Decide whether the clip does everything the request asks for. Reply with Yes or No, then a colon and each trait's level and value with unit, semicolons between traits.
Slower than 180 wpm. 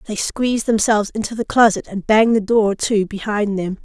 No: fast, 205 wpm